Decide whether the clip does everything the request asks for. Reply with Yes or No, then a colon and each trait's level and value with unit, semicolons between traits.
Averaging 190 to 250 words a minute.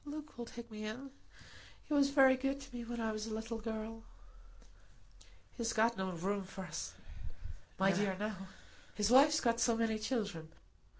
No: average, 175 wpm